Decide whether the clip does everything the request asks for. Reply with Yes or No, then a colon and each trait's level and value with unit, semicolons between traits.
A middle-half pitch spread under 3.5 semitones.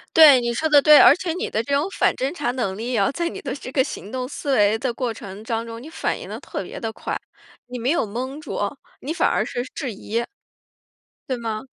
No: average, 3.9 semitones